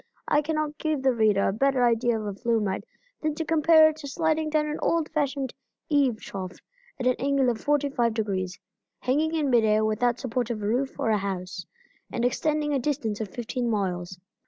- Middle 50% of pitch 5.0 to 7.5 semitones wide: Yes, wide, 5.4 semitones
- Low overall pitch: No, very high, 250 Hz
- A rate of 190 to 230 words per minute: Yes, average, 195 wpm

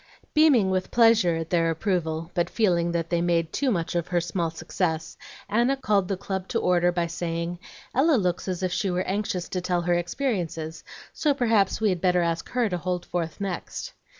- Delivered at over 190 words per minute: Yes, average, 200 wpm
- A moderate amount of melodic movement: Yes, average, 3.0 semitones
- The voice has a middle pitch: Yes, medium, 180 Hz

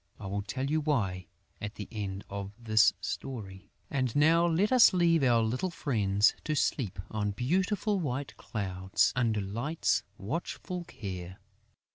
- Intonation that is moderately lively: No, wide, 7.4 semitones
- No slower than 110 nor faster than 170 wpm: Yes, average, 145 wpm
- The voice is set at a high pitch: No, low, 115 Hz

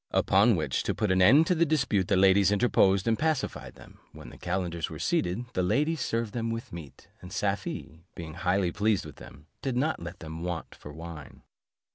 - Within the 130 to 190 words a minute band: No, average, 200 wpm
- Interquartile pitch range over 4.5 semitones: Yes, average, 5.2 semitones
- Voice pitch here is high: No, very low, 95 Hz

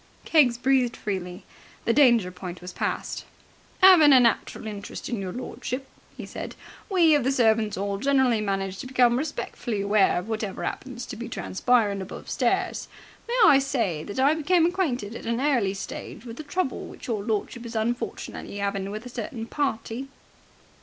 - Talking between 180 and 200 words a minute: No, average, 170 wpm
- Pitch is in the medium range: No, high, 235 Hz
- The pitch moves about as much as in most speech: Yes, average, 4.9 semitones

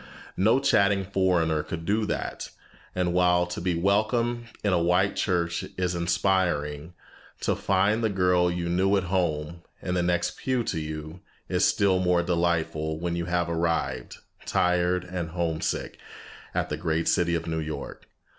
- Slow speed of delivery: No, average, 160 wpm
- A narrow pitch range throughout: Yes, narrow, 2.1 semitones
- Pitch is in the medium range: No, very low, 90 Hz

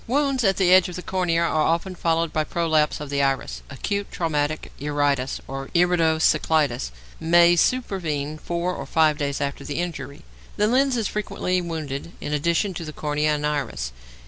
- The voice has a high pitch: No, medium, 160 Hz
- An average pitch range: Yes, average, 3.4 semitones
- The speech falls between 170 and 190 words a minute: Yes, average, 175 wpm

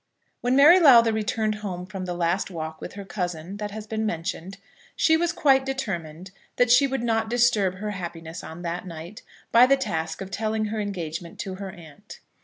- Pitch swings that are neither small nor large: Yes, average, 4.7 semitones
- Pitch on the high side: Yes, high, 200 Hz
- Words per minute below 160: No, average, 195 wpm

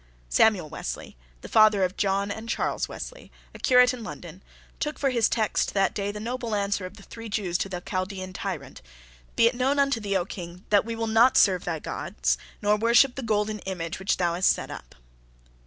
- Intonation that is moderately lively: Yes, average, 3.7 semitones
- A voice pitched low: No, high, 205 Hz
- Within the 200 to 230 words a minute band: Yes, fast, 205 wpm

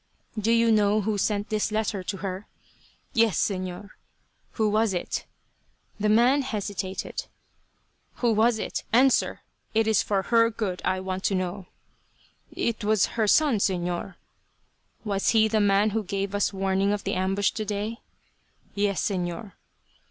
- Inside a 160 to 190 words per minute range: No, average, 145 wpm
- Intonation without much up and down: Yes, narrow, 2.3 semitones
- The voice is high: Yes, high, 205 Hz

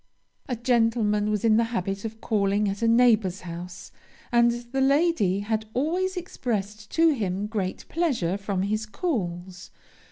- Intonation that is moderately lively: Yes, average, 3.7 semitones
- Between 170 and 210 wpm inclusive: No, average, 150 wpm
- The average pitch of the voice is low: No, high, 215 Hz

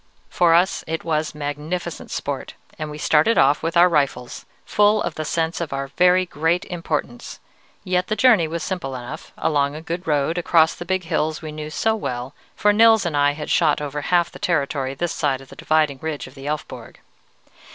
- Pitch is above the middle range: No, medium, 155 Hz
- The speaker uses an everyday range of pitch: Yes, average, 3.4 semitones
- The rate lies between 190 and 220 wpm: Yes, average, 200 wpm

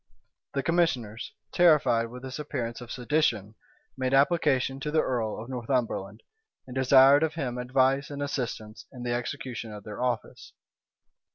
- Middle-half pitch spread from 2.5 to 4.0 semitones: Yes, average, 3.1 semitones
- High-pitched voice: No, low, 130 Hz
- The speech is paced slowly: No, average, 150 wpm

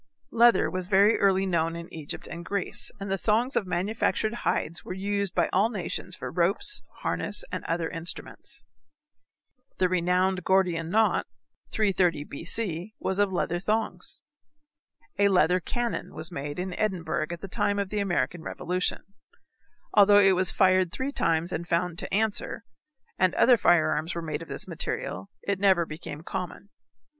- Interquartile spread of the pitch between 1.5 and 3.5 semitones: Yes, average, 3.0 semitones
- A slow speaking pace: No, average, 160 wpm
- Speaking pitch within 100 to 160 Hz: No, medium, 185 Hz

